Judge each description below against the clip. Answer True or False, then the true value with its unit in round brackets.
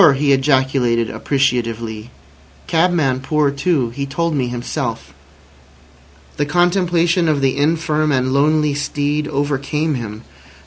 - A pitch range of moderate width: True (3.1 semitones)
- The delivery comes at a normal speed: False (115 wpm)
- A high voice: False (140 Hz)